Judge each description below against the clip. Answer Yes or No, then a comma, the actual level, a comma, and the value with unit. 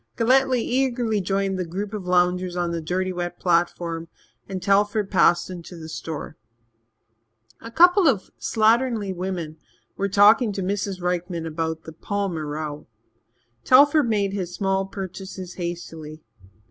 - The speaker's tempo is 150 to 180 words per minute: No, slow, 135 wpm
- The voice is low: No, medium, 185 Hz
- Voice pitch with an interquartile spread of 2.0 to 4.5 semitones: Yes, average, 3.1 semitones